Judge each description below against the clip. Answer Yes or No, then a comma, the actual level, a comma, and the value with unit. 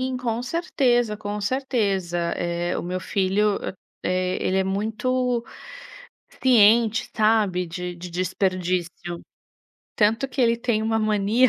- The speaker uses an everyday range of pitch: Yes, average, 4.3 semitones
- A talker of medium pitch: No, high, 210 Hz